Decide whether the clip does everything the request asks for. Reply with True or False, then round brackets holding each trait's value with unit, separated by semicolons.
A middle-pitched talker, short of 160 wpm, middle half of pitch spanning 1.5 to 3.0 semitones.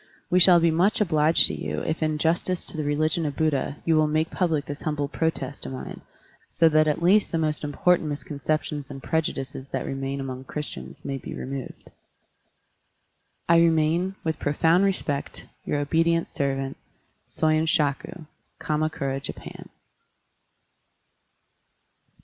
True (155 Hz; 140 wpm; 2.6 semitones)